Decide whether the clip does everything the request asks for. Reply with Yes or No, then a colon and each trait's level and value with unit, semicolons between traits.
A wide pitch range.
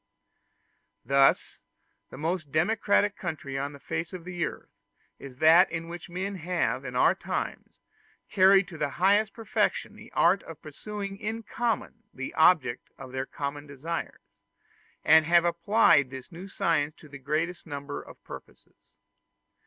No: average, 4.7 semitones